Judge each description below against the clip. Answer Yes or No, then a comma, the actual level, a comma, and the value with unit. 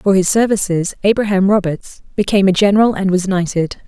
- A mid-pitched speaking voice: No, high, 195 Hz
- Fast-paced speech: No, average, 170 wpm